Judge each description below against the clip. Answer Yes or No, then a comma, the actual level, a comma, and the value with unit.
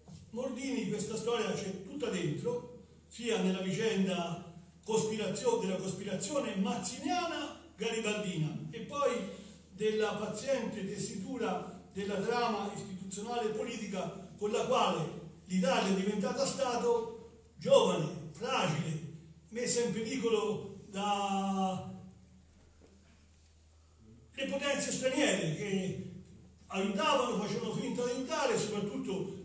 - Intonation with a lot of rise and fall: No, average, 4.1 semitones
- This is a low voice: No, high, 205 Hz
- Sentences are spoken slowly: Yes, slow, 95 wpm